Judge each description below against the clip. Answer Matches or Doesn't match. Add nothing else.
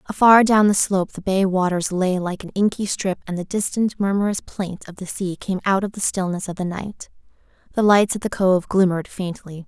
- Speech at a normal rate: Doesn't match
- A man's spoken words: Doesn't match